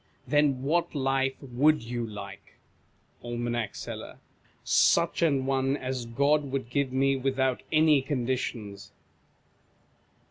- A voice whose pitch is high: No, low, 135 Hz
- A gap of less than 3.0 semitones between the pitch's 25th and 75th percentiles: Yes, narrow, 2.5 semitones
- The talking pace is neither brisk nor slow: No, slow, 115 wpm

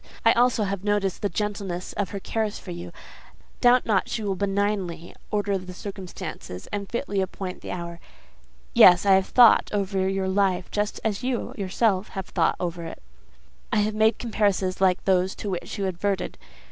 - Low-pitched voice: No, high, 195 Hz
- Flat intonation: Yes, narrow, 2.1 semitones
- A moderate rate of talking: Yes, average, 175 wpm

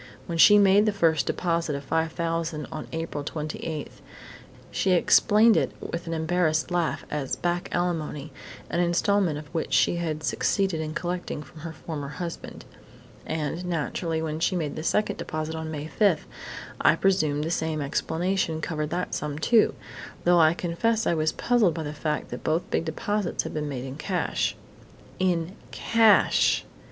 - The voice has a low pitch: No, medium, 165 Hz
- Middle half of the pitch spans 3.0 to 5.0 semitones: No, narrow, 2.5 semitones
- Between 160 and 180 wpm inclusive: Yes, average, 165 wpm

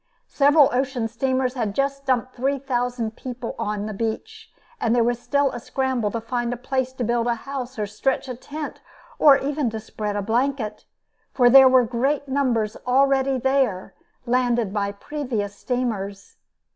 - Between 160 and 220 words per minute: Yes, average, 170 wpm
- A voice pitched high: Yes, very high, 250 Hz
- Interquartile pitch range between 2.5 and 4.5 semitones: Yes, average, 3.1 semitones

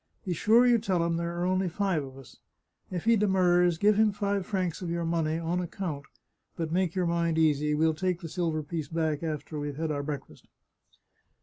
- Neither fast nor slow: No, fast, 210 wpm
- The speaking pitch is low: No, medium, 170 Hz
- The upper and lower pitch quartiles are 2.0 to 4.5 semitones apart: Yes, average, 2.9 semitones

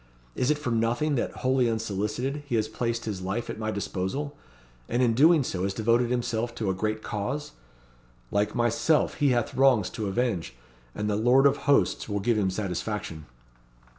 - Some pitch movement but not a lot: Yes, average, 3.4 semitones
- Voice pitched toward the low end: Yes, low, 115 Hz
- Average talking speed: Yes, average, 180 wpm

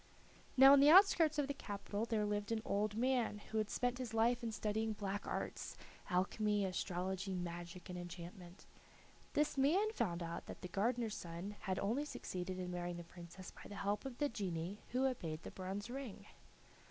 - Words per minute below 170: No, average, 185 wpm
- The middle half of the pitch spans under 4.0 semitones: No, average, 5.1 semitones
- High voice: Yes, high, 205 Hz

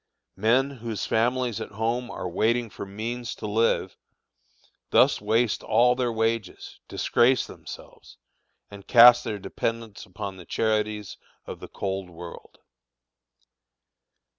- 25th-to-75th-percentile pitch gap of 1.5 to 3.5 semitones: Yes, average, 2.8 semitones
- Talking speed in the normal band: No, slow, 120 wpm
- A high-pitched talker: No, low, 115 Hz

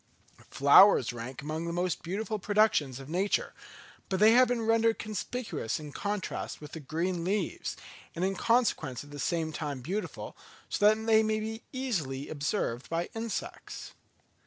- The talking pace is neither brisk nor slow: Yes, average, 160 wpm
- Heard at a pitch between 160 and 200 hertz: Yes, medium, 185 Hz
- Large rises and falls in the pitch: Yes, wide, 6.5 semitones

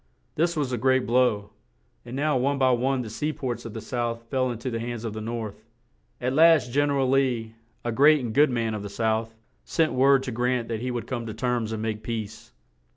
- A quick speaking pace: Yes, fast, 235 wpm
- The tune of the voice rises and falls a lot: No, average, 3.0 semitones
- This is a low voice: Yes, low, 125 Hz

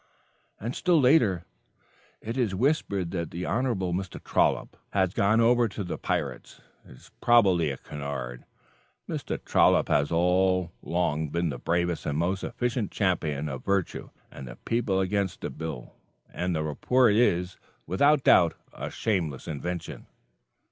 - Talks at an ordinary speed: Yes, average, 150 wpm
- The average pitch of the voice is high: No, very low, 90 Hz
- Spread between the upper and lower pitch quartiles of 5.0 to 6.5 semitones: Yes, average, 5.3 semitones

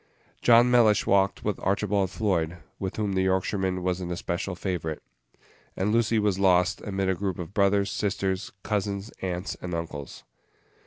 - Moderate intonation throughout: No, narrow, 2.1 semitones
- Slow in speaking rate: No, average, 155 wpm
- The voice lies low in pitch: Yes, very low, 95 Hz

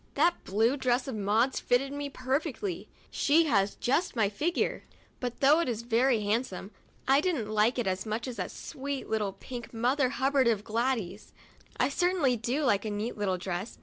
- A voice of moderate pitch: No, high, 245 Hz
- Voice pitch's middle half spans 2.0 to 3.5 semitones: No, average, 4.3 semitones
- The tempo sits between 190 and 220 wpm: No, average, 180 wpm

